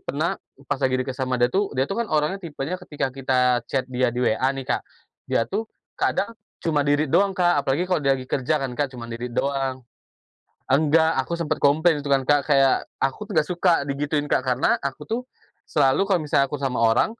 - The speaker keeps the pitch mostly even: No, average, 3.5 semitones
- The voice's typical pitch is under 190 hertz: Yes, medium, 140 Hz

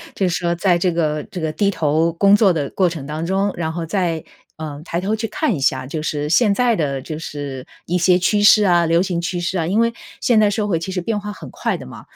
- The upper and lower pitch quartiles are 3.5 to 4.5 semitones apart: Yes, average, 4.0 semitones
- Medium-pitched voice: Yes, medium, 175 Hz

